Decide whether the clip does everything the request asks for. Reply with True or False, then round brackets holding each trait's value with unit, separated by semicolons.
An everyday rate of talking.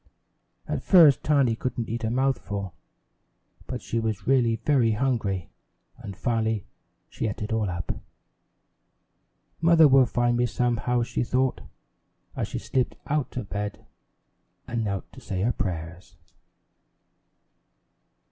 False (130 wpm)